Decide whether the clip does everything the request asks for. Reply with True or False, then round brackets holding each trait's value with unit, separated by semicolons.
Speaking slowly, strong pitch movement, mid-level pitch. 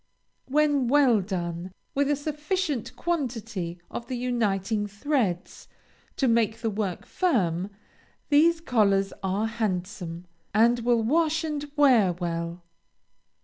False (115 wpm; 6.9 semitones; 225 Hz)